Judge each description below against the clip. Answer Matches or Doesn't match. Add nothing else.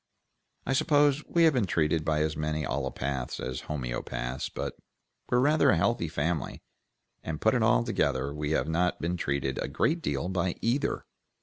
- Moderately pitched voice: Doesn't match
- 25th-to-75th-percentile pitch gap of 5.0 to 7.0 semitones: Matches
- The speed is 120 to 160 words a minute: Doesn't match